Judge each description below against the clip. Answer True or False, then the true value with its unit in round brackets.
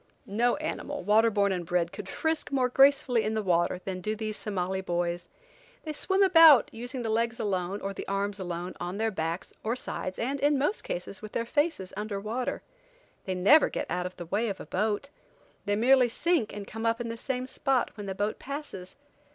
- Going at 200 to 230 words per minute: True (205 wpm)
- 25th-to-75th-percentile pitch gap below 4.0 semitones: False (5.0 semitones)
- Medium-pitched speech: False (215 Hz)